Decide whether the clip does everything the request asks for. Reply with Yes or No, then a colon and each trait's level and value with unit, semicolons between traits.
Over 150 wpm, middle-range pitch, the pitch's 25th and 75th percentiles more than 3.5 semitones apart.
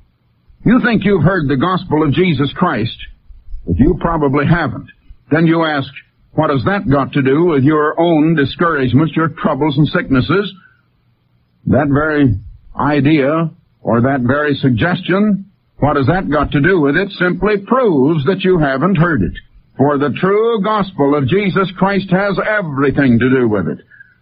Yes: average, 160 wpm; medium, 150 Hz; average, 5.0 semitones